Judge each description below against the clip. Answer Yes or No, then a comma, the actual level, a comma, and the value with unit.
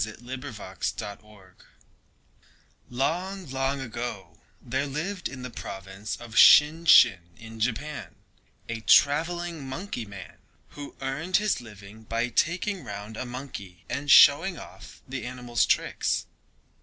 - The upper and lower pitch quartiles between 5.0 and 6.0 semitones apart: Yes, average, 5.3 semitones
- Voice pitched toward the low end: Yes, low, 125 Hz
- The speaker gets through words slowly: Yes, slow, 130 wpm